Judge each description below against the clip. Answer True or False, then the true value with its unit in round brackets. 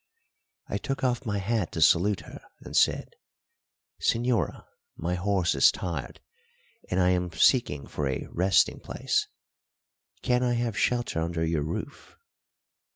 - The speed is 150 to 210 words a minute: False (140 wpm)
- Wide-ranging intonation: True (6.2 semitones)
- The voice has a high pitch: False (95 Hz)